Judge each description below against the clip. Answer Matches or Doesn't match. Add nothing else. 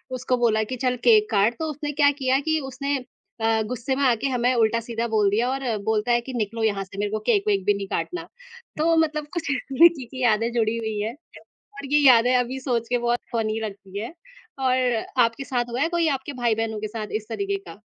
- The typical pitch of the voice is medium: Doesn't match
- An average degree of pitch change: Matches